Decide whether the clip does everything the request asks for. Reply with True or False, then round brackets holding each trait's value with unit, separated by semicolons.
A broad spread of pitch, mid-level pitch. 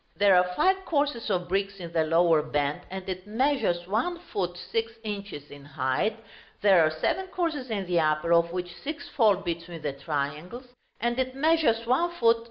False (6.5 semitones; 195 Hz)